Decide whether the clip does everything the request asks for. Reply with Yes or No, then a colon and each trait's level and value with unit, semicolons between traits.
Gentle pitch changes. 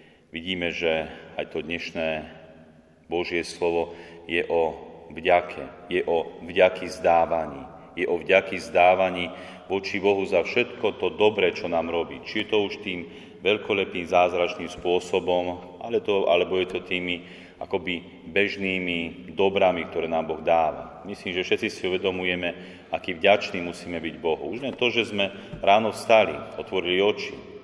Yes: narrow, 1.9 semitones